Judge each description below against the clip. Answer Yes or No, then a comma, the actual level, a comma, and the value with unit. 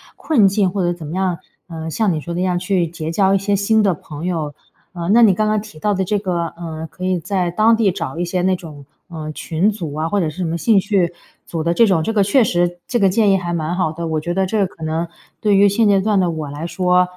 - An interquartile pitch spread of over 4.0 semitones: No, average, 3.3 semitones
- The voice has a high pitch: No, medium, 180 Hz